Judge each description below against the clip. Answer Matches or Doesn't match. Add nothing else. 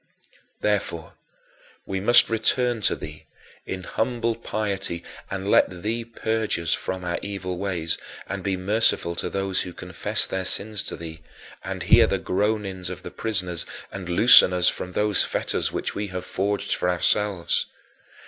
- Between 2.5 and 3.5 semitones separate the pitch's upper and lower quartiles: Matches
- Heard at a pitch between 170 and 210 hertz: Doesn't match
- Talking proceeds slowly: Doesn't match